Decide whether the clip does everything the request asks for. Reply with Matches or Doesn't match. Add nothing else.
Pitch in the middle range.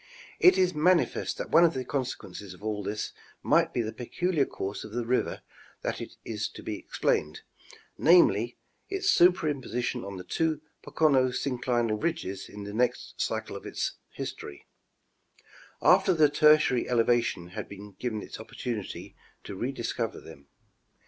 Doesn't match